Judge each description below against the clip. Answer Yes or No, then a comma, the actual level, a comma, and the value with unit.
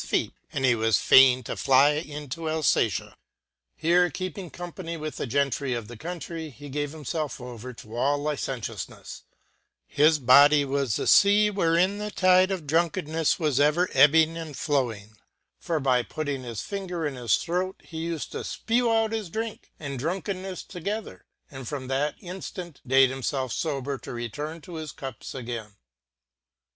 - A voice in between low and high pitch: Yes, medium, 150 Hz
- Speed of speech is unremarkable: Yes, average, 165 wpm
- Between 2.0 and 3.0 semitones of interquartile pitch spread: No, average, 4.7 semitones